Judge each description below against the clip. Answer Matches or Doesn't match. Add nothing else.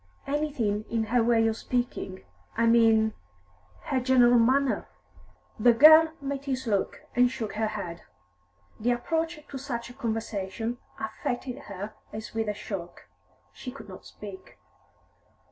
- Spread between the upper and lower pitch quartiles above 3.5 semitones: Doesn't match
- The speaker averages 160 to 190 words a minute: Doesn't match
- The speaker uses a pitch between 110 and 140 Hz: Doesn't match